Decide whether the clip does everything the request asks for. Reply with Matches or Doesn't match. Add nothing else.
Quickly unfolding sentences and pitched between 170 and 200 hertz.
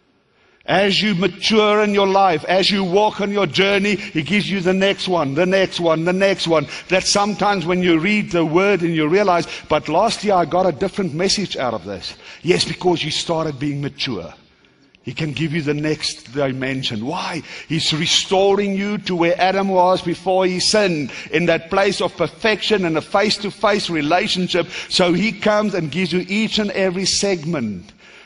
Doesn't match